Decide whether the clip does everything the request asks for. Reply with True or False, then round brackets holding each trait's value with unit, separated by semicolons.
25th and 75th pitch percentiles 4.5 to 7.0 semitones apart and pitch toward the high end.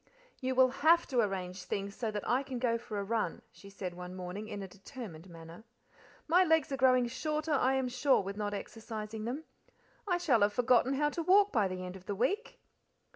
True (5.2 semitones; 230 Hz)